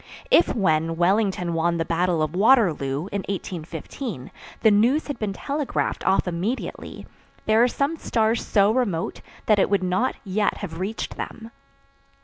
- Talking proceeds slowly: No, average, 150 wpm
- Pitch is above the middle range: Yes, high, 195 Hz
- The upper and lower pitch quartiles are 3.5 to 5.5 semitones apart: Yes, average, 4.9 semitones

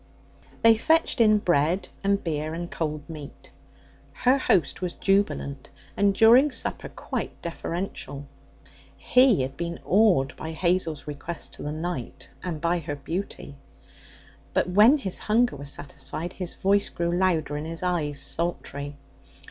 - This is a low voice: No, medium, 170 Hz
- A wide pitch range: No, average, 4.8 semitones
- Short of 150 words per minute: Yes, average, 140 wpm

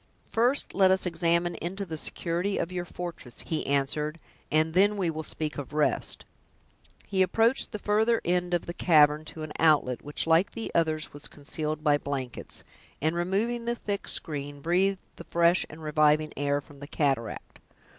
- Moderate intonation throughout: Yes, average, 3.7 semitones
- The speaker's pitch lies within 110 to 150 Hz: No, medium, 165 Hz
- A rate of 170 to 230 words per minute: Yes, average, 175 wpm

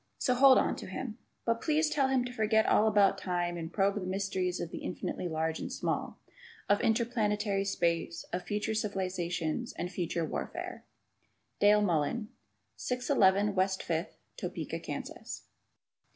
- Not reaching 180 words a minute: Yes, average, 150 wpm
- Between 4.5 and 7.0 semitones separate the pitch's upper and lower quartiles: No, average, 3.7 semitones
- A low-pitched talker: No, high, 200 Hz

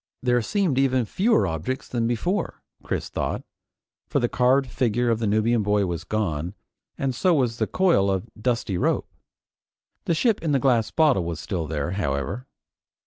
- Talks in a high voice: No, low, 120 Hz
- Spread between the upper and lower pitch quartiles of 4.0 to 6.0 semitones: Yes, wide, 5.5 semitones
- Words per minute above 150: Yes, average, 170 wpm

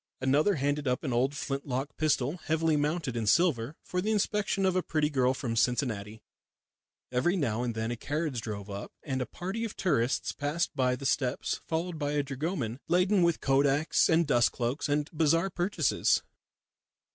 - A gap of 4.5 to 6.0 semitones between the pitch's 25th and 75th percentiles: Yes, average, 4.8 semitones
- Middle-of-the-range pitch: Yes, medium, 145 Hz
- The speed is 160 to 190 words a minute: Yes, average, 180 wpm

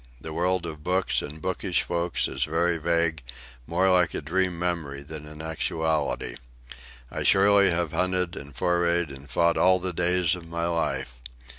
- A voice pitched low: Yes, very low, 85 Hz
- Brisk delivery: No, average, 165 wpm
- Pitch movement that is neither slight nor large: No, narrow, 2.2 semitones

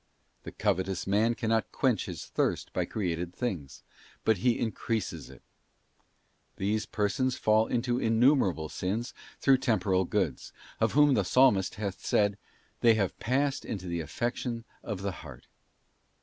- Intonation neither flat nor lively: Yes, average, 4.2 semitones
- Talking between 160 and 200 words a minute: No, average, 150 wpm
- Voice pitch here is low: Yes, low, 105 Hz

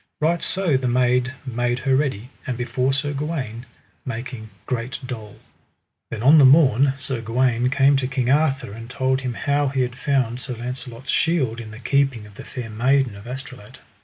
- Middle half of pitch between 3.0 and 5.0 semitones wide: No, narrow, 2.5 semitones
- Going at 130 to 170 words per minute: No, average, 185 wpm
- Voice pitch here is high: No, low, 125 Hz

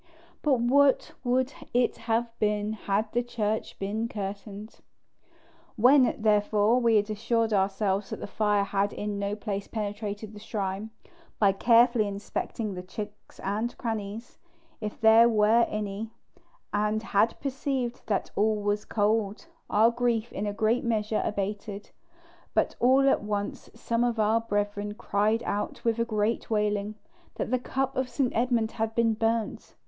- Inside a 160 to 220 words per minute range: No, average, 150 wpm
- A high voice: Yes, high, 215 Hz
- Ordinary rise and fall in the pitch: No, narrow, 2.1 semitones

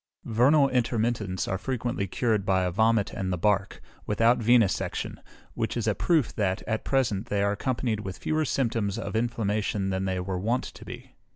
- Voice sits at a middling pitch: No, low, 110 Hz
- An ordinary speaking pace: Yes, average, 180 wpm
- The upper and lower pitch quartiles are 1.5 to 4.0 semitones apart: Yes, average, 3.7 semitones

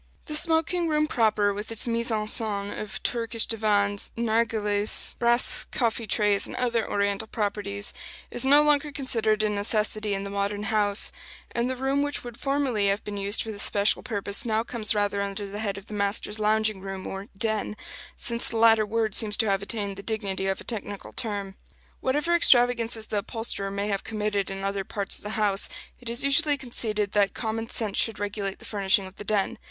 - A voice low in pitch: No, high, 215 Hz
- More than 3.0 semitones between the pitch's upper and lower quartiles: No, narrow, 2.5 semitones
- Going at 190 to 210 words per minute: Yes, average, 195 wpm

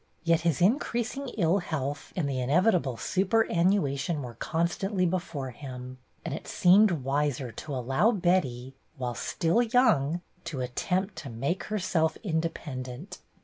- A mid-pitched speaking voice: Yes, medium, 160 Hz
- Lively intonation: Yes, wide, 5.7 semitones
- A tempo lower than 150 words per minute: Yes, average, 140 wpm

